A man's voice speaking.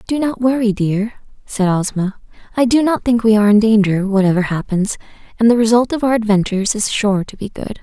No: female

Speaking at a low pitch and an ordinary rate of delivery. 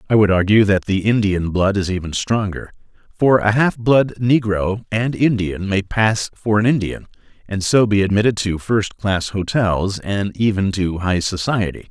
Yes: low, 105 Hz; average, 170 wpm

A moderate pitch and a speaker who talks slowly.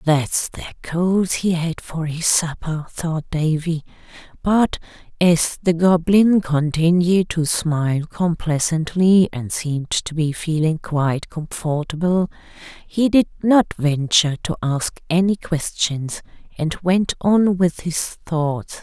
Yes: medium, 165 Hz; slow, 125 wpm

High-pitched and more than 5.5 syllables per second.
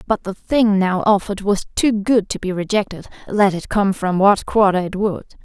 No: high, 200 Hz; 4.9 syllables/s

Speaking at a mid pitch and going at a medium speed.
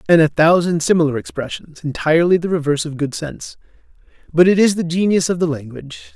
Yes: medium, 165 Hz; average, 185 wpm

